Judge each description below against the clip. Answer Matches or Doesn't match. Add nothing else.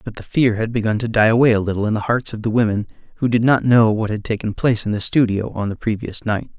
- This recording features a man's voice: Matches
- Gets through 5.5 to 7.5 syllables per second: Matches